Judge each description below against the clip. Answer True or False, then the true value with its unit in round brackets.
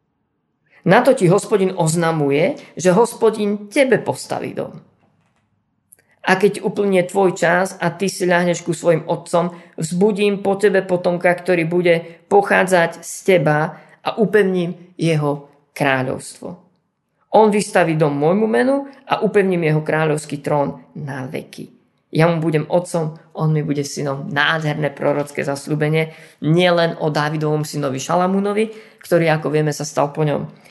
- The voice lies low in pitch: False (170 Hz)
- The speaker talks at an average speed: True (135 wpm)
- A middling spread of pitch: True (3.7 semitones)